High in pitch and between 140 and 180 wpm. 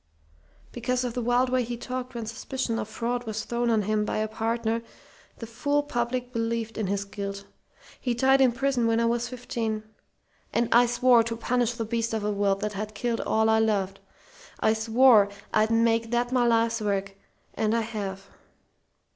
No: high, 230 Hz; average, 190 wpm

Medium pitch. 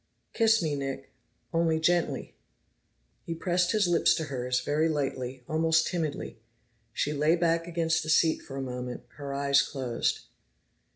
Yes: medium, 155 Hz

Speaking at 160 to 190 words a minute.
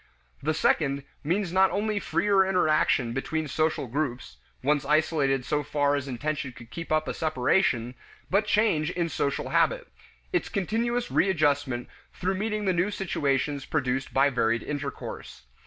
No: average, 145 wpm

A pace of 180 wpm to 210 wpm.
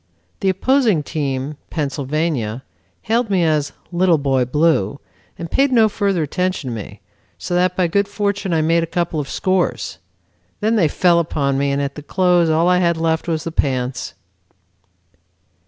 No: average, 170 wpm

